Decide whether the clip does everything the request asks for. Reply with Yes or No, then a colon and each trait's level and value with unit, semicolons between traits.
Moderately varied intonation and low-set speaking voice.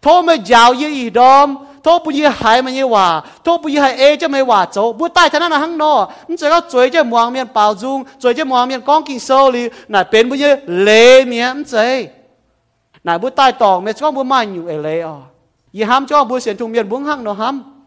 No: average, 4.7 semitones; very high, 255 Hz